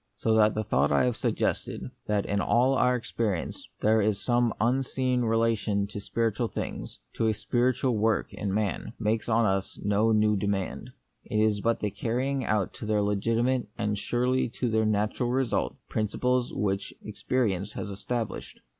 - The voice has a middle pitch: No, low, 110 Hz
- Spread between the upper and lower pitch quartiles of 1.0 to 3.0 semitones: Yes, average, 2.7 semitones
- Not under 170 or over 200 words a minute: Yes, average, 175 wpm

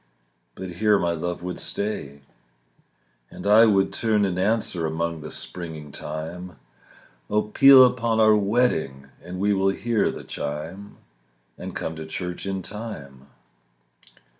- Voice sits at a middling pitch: No, very low, 95 Hz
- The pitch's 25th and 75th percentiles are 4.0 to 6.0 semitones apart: Yes, average, 4.7 semitones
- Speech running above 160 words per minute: No, average, 140 wpm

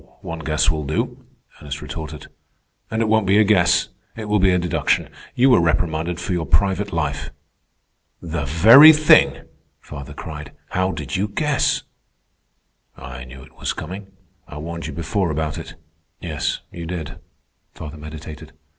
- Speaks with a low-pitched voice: Yes, very low, 85 Hz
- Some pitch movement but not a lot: Yes, average, 4.2 semitones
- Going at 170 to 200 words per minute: No, average, 155 wpm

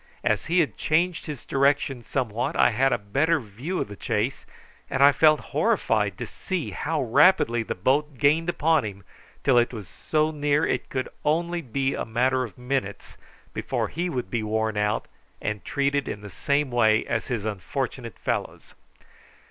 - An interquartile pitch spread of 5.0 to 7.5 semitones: Yes, average, 5.3 semitones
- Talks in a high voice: No, low, 135 Hz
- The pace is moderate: Yes, average, 180 wpm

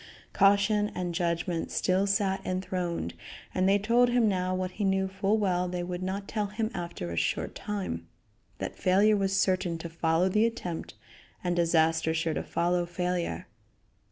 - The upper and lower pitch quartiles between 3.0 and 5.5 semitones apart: No, narrow, 2.5 semitones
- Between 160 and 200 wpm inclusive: Yes, average, 165 wpm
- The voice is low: No, medium, 185 Hz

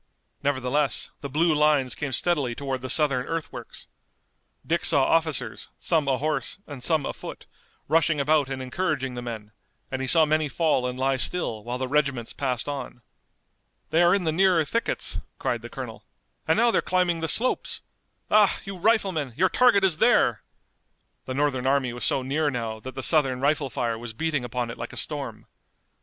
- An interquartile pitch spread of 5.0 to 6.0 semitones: No, average, 4.1 semitones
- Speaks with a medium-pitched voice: Yes, medium, 145 Hz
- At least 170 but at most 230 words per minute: Yes, average, 180 wpm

